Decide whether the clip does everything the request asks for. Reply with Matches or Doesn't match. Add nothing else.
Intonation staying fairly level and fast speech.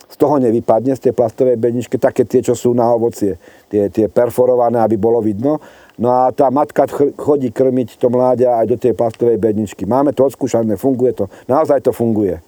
Matches